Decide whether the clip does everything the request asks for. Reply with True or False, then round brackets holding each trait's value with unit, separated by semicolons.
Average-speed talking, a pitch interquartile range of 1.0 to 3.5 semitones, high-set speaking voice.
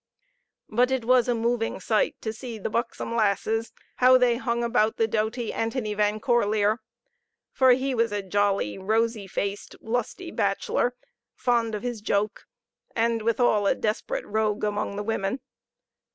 True (150 wpm; 2.4 semitones; 225 Hz)